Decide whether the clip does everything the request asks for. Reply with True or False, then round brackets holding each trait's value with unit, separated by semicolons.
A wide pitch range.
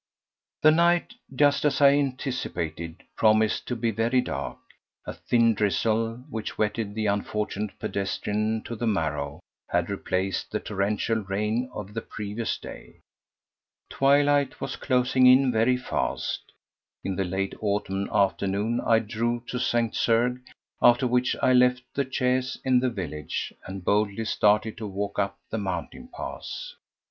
False (3.9 semitones)